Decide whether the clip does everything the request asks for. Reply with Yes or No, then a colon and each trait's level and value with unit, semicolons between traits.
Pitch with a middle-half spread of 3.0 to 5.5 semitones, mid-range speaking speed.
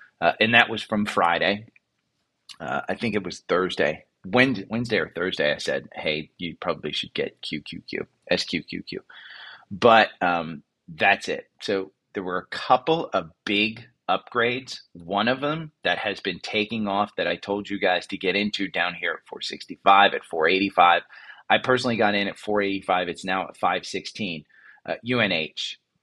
Yes: average, 3.5 semitones; average, 180 wpm